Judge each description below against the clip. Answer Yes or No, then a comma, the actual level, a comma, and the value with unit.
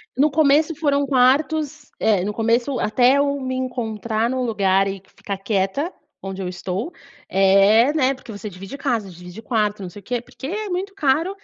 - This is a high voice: Yes, high, 240 Hz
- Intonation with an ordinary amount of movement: No, wide, 6.1 semitones